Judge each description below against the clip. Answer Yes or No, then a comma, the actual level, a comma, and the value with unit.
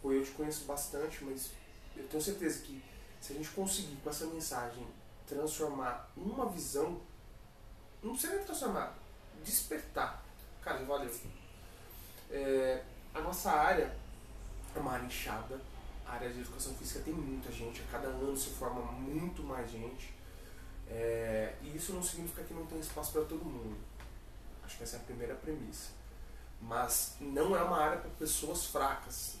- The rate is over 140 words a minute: Yes, average, 155 wpm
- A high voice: No, low, 130 Hz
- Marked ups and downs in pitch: Yes, wide, 5.8 semitones